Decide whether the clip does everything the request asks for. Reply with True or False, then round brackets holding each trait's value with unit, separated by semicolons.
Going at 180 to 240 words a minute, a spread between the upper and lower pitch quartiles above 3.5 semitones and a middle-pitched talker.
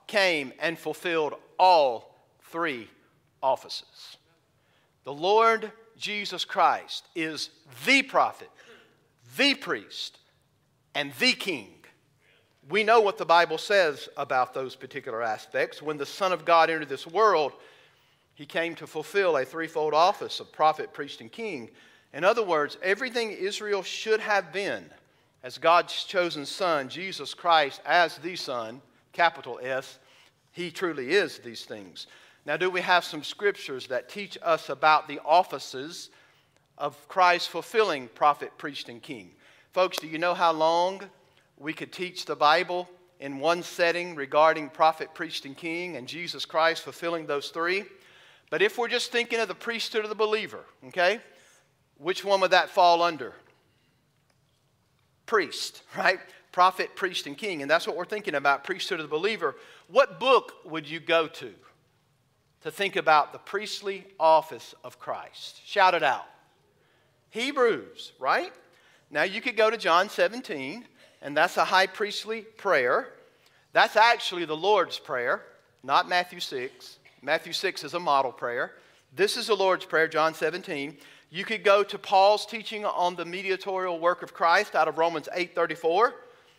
False (150 wpm; 4.8 semitones; 175 Hz)